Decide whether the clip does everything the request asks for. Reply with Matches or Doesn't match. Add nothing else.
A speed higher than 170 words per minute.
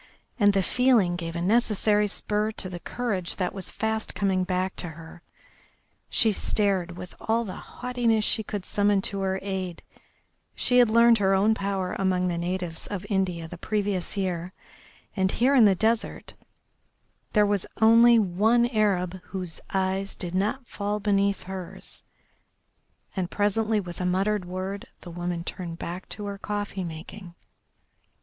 Doesn't match